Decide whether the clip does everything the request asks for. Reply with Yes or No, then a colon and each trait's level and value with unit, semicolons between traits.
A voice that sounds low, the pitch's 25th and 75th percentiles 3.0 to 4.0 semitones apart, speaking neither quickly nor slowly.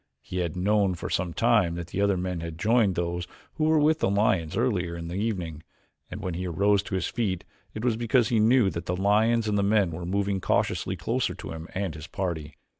No: very low, 95 Hz; average, 3.7 semitones; fast, 225 wpm